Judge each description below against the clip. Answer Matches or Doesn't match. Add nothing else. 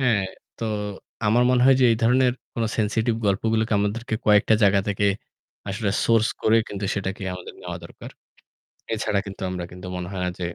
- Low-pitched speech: Matches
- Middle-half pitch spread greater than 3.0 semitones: Doesn't match